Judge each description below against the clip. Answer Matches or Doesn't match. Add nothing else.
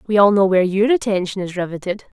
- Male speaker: Doesn't match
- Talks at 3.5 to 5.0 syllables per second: Doesn't match